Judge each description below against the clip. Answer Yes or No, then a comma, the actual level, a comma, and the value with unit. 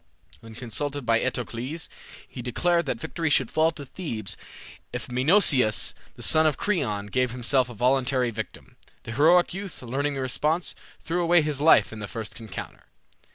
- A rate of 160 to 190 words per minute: Yes, average, 165 wpm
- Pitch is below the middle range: Yes, low, 130 Hz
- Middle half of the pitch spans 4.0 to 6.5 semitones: Yes, average, 5.2 semitones